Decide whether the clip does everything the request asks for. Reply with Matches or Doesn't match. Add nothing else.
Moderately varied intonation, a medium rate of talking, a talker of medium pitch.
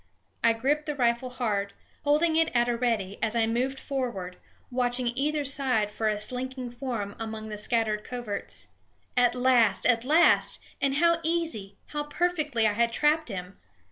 Doesn't match